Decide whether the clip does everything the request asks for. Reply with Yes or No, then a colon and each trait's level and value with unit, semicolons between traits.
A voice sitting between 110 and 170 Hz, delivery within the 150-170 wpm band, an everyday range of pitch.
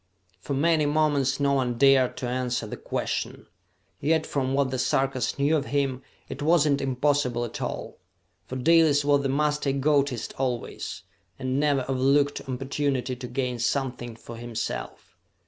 No: low, 135 Hz; average, 155 wpm; narrow, 2.2 semitones